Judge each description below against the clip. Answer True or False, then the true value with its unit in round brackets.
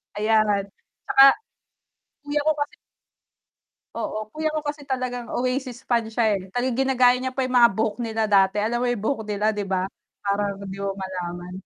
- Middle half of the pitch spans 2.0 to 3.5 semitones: False (4.1 semitones)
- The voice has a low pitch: False (225 Hz)